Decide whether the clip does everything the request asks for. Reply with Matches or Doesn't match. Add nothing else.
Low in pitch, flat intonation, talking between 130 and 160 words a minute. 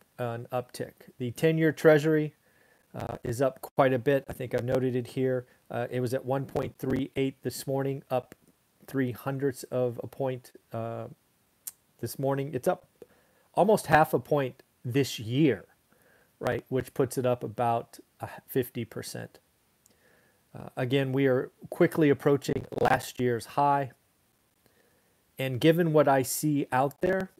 Matches